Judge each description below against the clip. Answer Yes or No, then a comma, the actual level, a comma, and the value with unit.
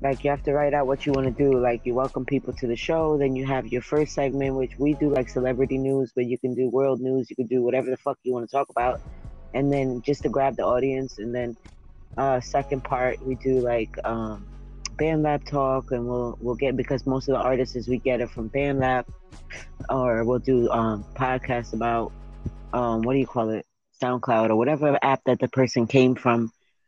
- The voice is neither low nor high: No, low, 130 Hz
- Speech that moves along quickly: Yes, fast, 230 wpm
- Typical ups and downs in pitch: No, narrow, 2.0 semitones